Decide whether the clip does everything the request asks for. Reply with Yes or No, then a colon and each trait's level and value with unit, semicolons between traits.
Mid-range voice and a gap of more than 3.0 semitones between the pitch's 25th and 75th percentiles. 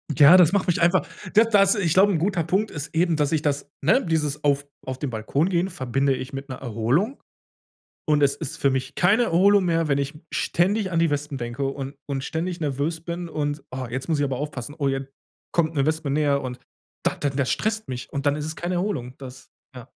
Yes: medium, 150 Hz; average, 4.1 semitones